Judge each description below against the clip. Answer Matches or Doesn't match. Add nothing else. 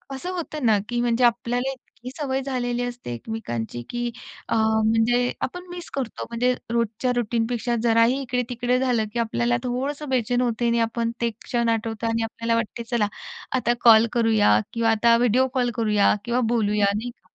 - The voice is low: Doesn't match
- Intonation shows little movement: Matches